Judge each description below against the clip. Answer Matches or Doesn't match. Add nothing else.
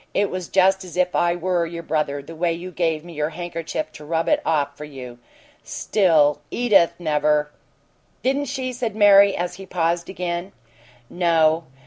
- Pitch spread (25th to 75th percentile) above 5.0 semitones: Doesn't match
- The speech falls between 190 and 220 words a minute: Doesn't match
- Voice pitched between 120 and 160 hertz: Doesn't match